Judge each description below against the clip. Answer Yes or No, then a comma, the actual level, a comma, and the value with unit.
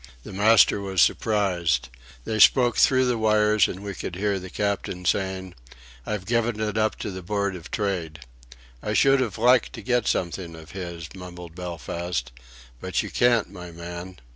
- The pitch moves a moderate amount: Yes, average, 3.6 semitones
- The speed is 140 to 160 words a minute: No, average, 170 wpm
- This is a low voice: Yes, very low, 95 Hz